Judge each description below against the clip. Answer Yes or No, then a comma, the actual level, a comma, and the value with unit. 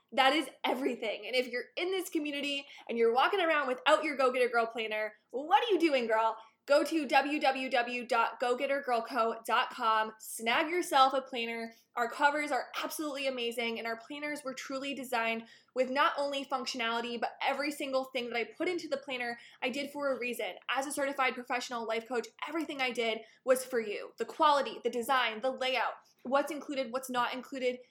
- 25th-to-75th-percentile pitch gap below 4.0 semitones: Yes, average, 3.2 semitones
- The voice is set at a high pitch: Yes, very high, 260 Hz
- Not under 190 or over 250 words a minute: No, average, 180 wpm